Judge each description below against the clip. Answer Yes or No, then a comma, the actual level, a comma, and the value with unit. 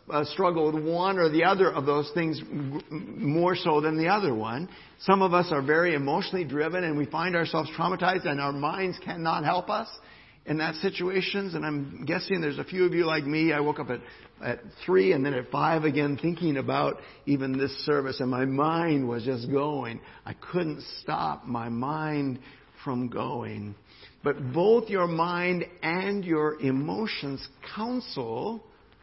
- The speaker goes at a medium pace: Yes, average, 170 wpm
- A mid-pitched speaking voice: Yes, medium, 155 Hz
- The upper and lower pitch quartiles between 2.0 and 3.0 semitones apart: No, average, 3.8 semitones